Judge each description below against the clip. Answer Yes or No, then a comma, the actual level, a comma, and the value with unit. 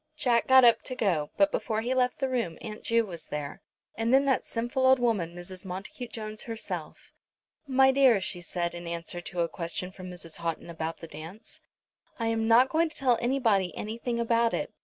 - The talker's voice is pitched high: Yes, high, 225 Hz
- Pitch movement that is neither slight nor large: No, wide, 6.0 semitones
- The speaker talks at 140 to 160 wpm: No, average, 200 wpm